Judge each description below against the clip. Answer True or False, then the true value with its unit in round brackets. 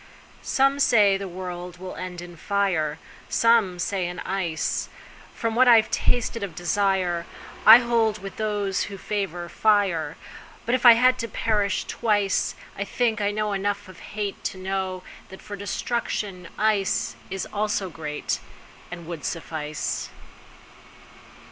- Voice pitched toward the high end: True (195 Hz)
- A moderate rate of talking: False (120 wpm)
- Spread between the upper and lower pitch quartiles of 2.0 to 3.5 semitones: True (3.2 semitones)